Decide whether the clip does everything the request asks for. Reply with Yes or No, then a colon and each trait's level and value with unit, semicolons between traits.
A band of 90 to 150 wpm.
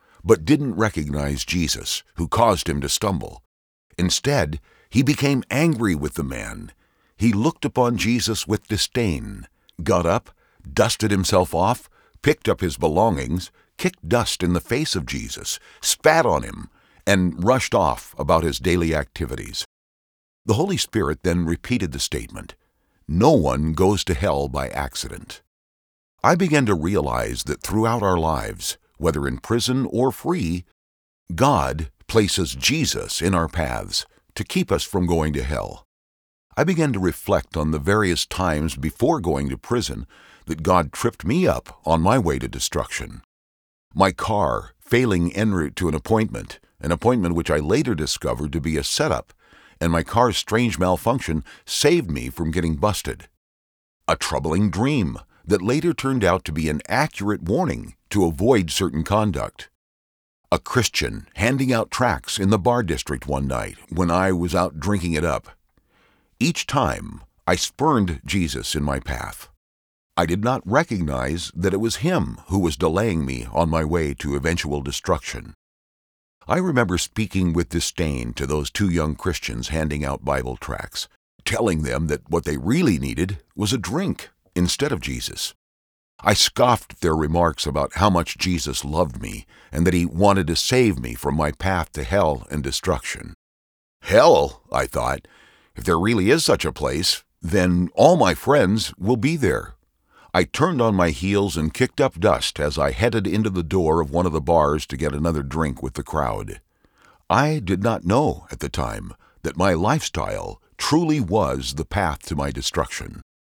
No: average, 165 wpm